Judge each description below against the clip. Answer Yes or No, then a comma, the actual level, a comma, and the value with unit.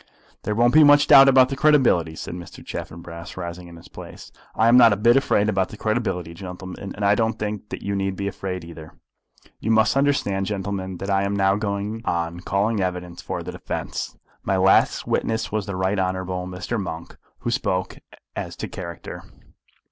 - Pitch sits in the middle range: No, low, 100 Hz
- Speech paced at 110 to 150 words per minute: No, average, 195 wpm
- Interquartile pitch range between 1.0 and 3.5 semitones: Yes, average, 3.1 semitones